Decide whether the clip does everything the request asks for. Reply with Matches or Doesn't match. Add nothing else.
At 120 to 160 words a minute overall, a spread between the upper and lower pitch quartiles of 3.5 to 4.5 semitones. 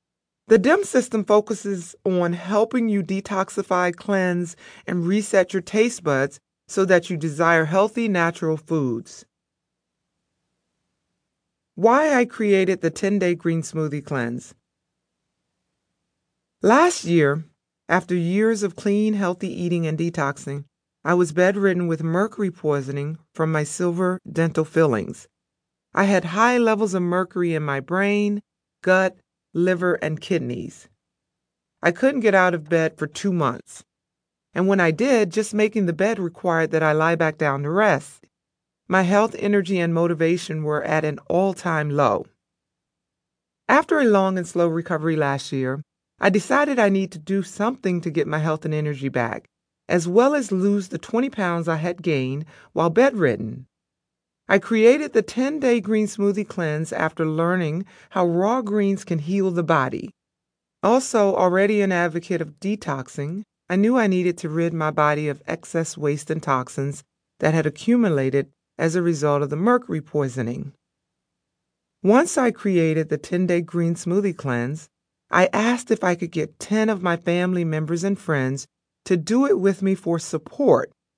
Matches